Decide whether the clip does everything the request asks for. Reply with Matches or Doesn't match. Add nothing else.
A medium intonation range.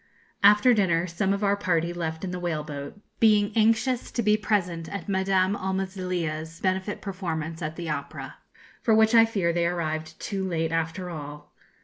Matches